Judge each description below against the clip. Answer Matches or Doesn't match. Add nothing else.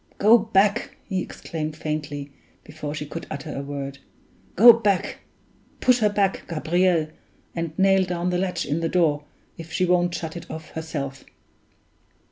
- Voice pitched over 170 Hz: Doesn't match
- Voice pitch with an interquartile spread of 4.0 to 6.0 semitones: Doesn't match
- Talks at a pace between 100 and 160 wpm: Matches